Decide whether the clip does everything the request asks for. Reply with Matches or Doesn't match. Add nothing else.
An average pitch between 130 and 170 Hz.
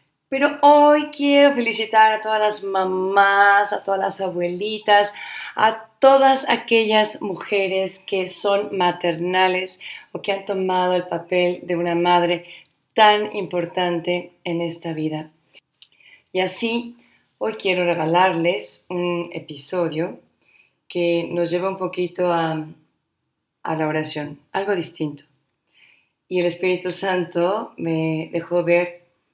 Doesn't match